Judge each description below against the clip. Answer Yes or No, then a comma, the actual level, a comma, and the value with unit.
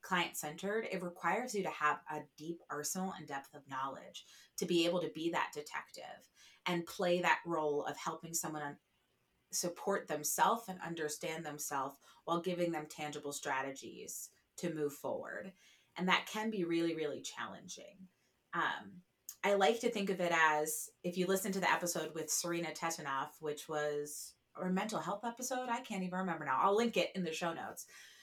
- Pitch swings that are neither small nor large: Yes, average, 3.8 semitones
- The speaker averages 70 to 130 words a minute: No, average, 175 wpm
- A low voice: No, medium, 170 Hz